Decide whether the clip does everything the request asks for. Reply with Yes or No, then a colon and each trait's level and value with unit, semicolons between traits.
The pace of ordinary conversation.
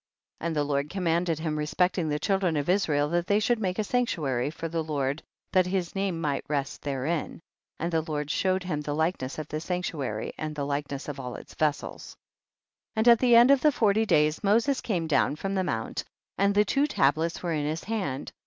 No: fast, 215 wpm